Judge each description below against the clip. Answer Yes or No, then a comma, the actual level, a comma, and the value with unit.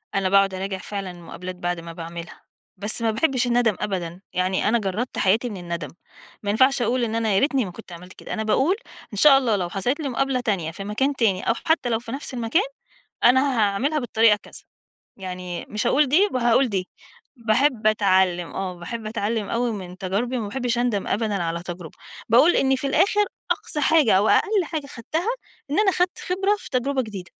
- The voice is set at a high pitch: Yes, high, 225 Hz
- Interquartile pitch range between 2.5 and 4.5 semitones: No, wide, 5.6 semitones